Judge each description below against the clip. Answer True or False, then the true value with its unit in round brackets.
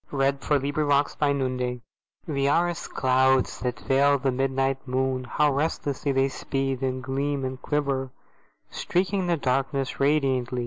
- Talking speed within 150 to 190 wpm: False (140 wpm)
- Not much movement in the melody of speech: True (1.6 semitones)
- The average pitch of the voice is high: False (135 Hz)